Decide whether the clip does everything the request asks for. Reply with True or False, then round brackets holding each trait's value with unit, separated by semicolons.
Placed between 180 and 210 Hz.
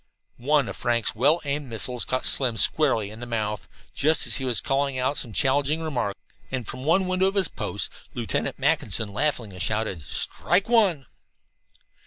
False (130 Hz)